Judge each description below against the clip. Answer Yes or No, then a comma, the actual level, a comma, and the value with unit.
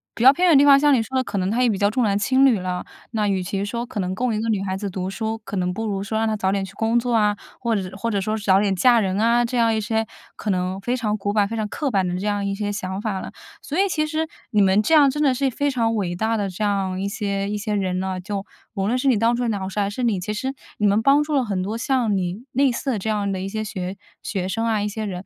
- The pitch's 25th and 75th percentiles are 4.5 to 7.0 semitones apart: No, average, 3.4 semitones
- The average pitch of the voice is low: No, high, 210 Hz